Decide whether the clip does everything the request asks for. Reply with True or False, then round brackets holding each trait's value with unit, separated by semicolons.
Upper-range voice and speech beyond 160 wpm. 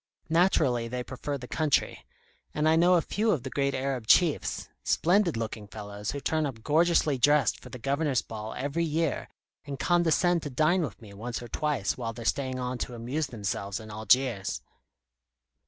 False (135 Hz; 180 wpm)